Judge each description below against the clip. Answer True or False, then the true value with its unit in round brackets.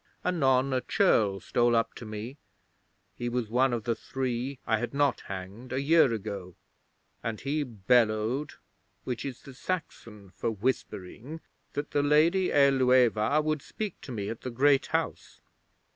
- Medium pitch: False (125 Hz)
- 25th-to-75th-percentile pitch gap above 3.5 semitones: True (4.0 semitones)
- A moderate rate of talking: True (155 wpm)